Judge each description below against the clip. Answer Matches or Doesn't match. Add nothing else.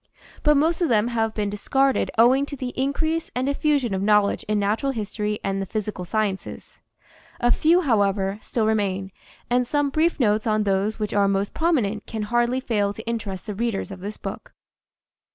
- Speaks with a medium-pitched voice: Doesn't match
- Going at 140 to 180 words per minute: Doesn't match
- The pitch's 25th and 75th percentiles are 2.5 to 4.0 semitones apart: Doesn't match